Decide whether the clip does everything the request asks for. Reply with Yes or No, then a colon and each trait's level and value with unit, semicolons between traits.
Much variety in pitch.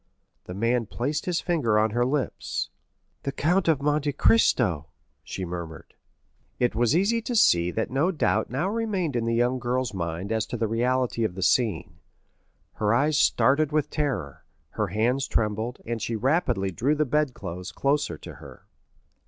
Yes: wide, 5.7 semitones